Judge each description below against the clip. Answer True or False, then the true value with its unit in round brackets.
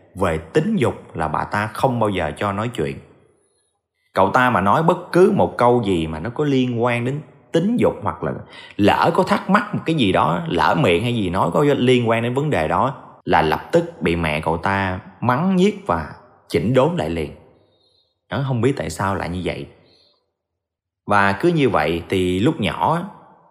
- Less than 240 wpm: True (205 wpm)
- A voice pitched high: False (110 Hz)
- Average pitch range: False (7.0 semitones)